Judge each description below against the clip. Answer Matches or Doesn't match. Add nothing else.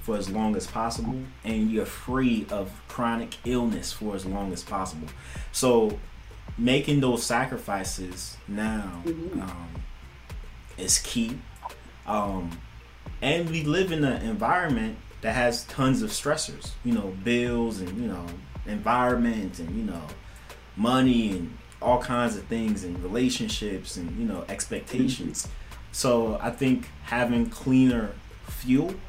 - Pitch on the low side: Matches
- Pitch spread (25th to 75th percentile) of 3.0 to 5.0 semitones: Matches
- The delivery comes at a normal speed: Doesn't match